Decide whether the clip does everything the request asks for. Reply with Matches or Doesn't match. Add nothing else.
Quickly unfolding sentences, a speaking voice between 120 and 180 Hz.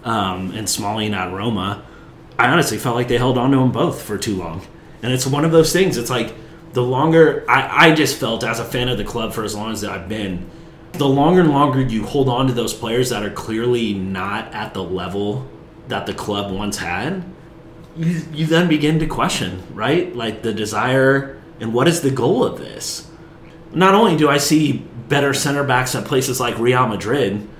Matches